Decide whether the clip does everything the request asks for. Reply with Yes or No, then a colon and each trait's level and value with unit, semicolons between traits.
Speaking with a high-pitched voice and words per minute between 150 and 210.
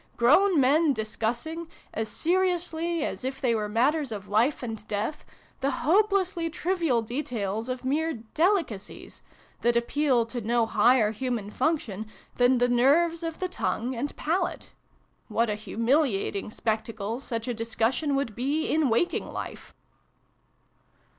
No: very high, 255 Hz; average, 140 wpm